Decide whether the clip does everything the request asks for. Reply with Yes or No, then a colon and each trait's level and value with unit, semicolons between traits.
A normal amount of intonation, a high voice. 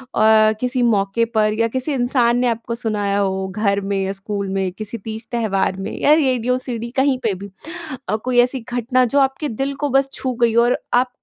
Yes: average, 3.8 semitones; high, 230 Hz